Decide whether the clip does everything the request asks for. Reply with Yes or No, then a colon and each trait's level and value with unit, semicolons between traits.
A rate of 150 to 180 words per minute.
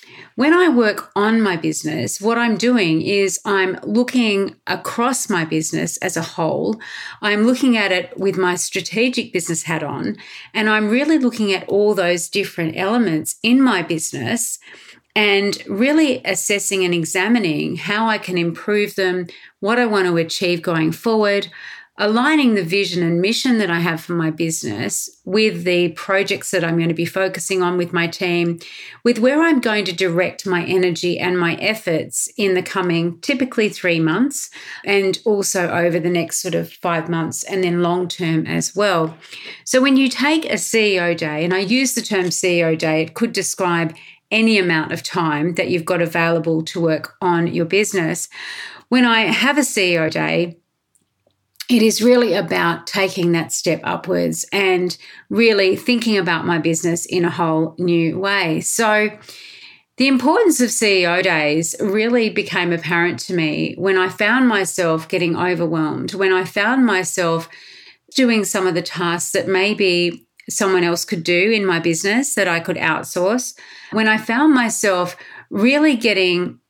Yes: average, 165 wpm